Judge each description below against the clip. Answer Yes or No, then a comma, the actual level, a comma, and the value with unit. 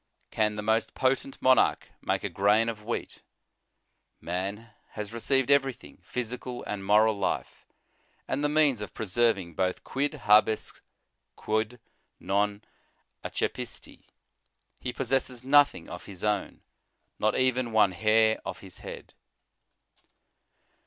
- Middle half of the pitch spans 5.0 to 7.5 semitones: No, average, 3.7 semitones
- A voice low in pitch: Yes, low, 110 Hz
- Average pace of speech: No, slow, 120 wpm